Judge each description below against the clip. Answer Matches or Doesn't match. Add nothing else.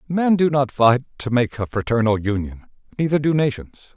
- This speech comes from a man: Matches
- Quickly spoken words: Doesn't match